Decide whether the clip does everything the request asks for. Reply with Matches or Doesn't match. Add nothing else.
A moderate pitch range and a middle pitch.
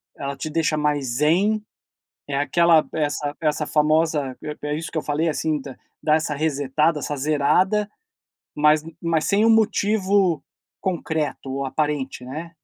Doesn't match